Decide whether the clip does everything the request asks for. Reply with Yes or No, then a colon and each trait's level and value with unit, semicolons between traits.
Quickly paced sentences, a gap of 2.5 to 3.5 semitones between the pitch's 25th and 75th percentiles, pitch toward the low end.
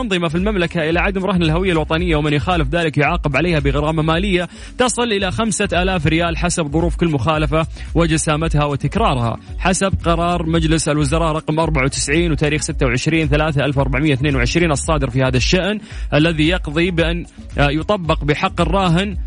No: fast, 150 wpm; average, 2.8 semitones; medium, 160 Hz